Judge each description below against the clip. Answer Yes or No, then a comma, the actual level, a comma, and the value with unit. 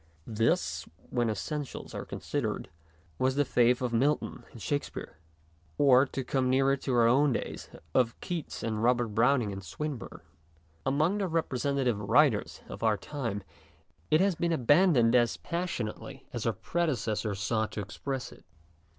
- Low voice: Yes, low, 125 Hz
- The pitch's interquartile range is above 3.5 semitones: Yes, average, 4.2 semitones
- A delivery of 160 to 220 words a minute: Yes, average, 170 wpm